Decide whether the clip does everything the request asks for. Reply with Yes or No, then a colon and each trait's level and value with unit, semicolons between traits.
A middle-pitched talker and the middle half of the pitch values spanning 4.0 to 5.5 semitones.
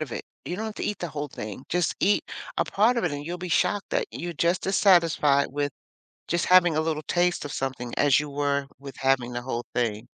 Yes: medium, 150 Hz; average, 4.5 semitones